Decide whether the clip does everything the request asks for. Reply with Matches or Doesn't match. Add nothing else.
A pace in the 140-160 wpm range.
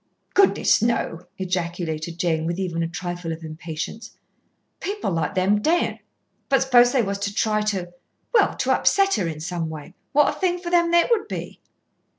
Doesn't match